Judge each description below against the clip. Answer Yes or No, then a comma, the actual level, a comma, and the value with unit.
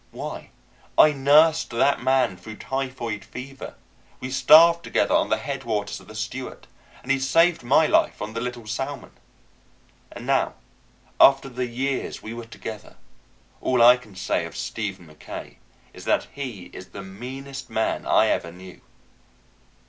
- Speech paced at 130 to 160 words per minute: Yes, average, 155 wpm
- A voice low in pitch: Yes, low, 125 Hz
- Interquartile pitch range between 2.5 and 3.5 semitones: No, average, 4.0 semitones